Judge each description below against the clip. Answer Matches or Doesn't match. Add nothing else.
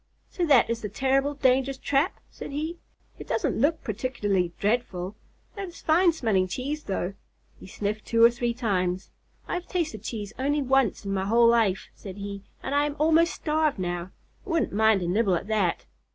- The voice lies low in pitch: Doesn't match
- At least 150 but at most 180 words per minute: Doesn't match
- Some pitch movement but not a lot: Doesn't match